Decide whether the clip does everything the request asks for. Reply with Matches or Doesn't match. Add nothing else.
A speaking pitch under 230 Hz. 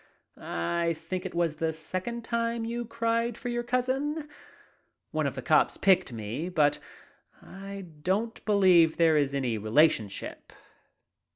Matches